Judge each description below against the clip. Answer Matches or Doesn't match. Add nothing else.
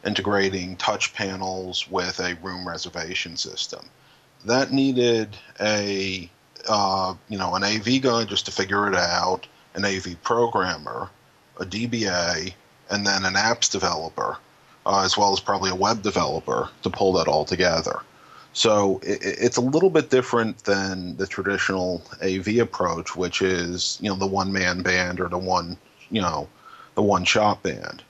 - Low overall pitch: Matches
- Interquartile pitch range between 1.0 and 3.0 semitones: Matches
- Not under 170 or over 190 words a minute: Doesn't match